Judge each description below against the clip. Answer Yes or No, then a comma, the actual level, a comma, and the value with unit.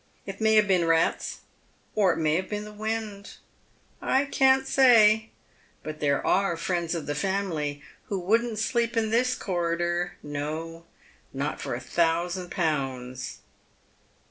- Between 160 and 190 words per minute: No, average, 145 wpm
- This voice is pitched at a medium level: Yes, medium, 180 Hz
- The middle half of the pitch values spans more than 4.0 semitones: Yes, average, 4.9 semitones